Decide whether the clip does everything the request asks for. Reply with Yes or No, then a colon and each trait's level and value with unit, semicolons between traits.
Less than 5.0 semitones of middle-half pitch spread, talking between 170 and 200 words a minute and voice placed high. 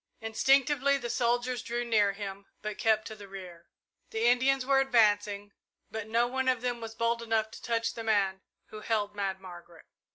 Yes: average, 2.9 semitones; average, 185 wpm; high, 225 Hz